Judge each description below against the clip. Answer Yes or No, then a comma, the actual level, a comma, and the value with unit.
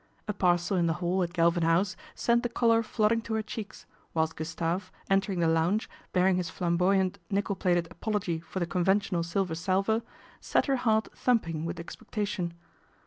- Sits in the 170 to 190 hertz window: Yes, medium, 185 Hz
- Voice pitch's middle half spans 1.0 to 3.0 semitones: No, average, 3.6 semitones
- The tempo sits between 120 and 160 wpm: No, average, 175 wpm